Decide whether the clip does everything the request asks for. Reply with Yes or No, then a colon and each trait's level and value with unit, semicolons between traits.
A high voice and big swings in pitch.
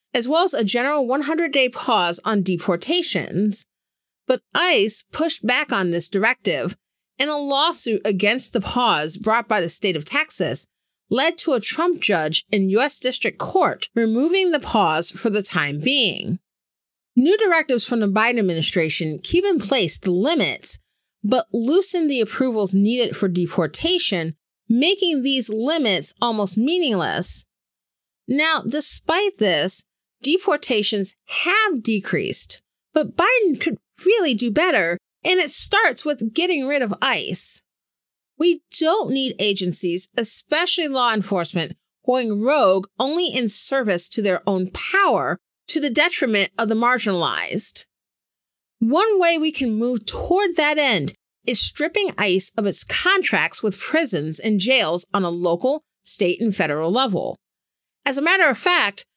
Yes: high, 245 Hz; wide, 7.5 semitones